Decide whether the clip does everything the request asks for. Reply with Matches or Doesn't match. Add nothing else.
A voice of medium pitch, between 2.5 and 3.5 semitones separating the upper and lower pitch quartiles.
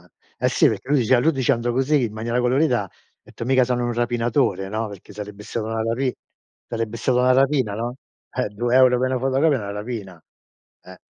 Doesn't match